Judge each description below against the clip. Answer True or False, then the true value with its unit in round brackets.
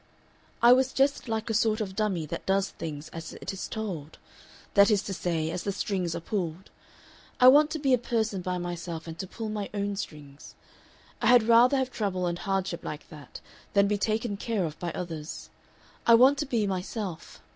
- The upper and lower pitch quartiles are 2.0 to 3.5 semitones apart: False (4.6 semitones)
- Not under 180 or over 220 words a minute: True (200 wpm)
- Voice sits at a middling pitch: False (200 Hz)